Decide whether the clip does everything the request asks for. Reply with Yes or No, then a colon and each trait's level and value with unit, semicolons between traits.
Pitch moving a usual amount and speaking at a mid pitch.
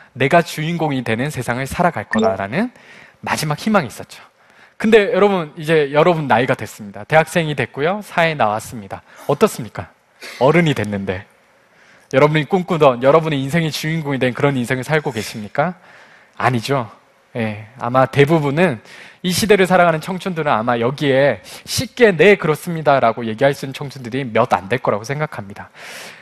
No: wide, 5.8 semitones; medium, 145 Hz